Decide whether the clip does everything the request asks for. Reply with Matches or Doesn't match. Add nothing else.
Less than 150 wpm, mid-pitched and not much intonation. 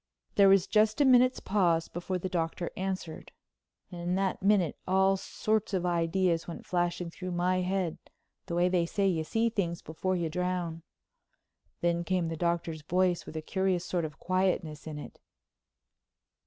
Doesn't match